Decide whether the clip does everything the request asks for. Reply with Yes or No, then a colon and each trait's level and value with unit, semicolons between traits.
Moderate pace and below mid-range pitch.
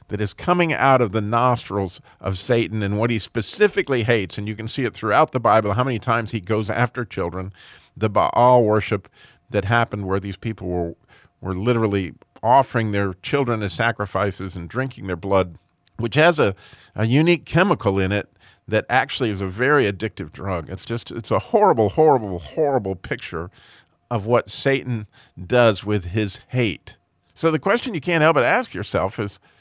Yes: average, 180 wpm; low, 110 Hz